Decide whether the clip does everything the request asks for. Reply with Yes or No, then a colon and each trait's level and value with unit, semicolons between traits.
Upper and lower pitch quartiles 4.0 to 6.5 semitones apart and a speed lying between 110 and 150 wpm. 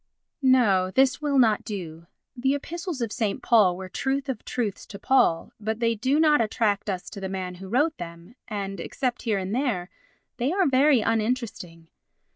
No: wide, 5.5 semitones; average, 180 wpm